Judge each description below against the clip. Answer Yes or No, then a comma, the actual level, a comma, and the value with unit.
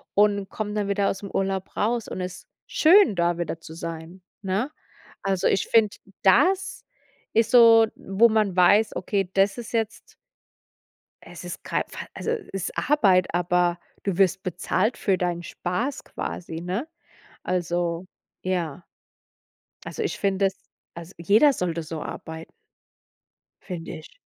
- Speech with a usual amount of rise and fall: Yes, average, 3.5 semitones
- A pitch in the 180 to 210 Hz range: Yes, high, 190 Hz